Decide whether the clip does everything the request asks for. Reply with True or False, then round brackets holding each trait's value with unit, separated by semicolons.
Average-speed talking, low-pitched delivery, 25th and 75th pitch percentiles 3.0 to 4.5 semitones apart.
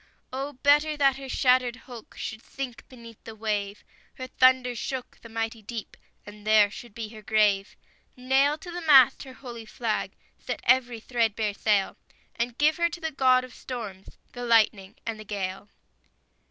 False (170 wpm; 235 Hz; 3.3 semitones)